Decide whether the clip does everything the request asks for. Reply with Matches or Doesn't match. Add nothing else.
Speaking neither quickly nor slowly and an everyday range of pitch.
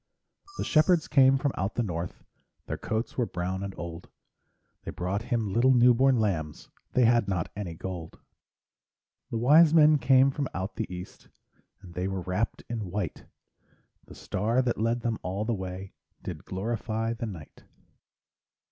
Matches